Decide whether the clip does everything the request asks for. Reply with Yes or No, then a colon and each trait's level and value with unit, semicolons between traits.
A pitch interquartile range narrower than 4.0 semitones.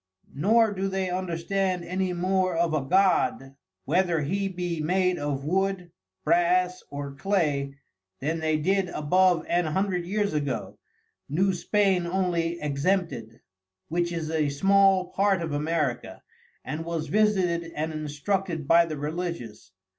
Yes: average, 3.5 semitones